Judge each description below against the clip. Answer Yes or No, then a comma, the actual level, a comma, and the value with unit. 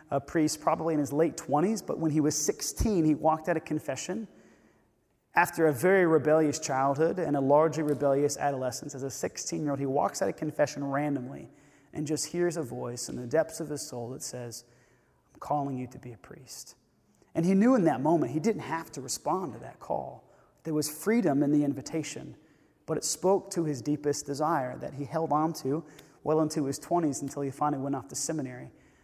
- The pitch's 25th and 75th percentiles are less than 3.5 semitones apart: Yes, narrow, 2.4 semitones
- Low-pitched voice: No, medium, 150 Hz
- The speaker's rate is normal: No, fast, 210 wpm